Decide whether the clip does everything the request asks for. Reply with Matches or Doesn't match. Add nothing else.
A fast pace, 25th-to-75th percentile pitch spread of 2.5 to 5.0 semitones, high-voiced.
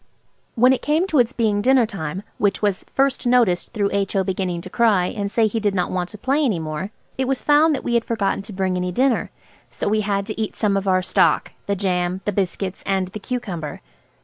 Matches